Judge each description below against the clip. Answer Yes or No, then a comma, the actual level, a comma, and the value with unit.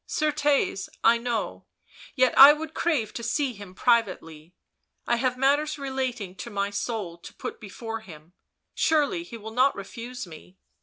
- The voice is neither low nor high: No, high, 235 Hz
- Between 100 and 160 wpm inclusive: No, average, 170 wpm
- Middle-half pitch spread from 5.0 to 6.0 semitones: Yes, wide, 5.4 semitones